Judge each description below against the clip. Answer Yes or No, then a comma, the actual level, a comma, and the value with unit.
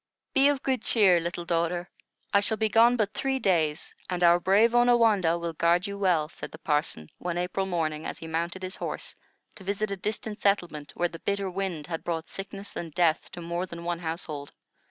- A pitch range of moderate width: Yes, average, 3.2 semitones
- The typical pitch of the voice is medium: Yes, medium, 180 Hz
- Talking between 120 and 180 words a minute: No, fast, 205 wpm